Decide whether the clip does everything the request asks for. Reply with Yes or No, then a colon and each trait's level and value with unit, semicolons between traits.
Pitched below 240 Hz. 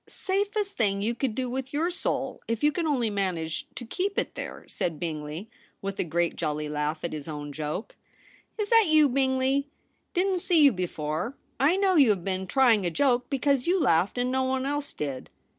No: high, 245 Hz